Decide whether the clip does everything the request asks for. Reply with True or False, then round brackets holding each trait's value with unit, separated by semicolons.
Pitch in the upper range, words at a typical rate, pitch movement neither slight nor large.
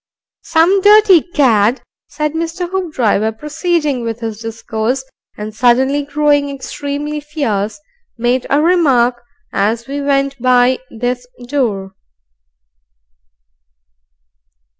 False (270 Hz; 95 wpm; 4.4 semitones)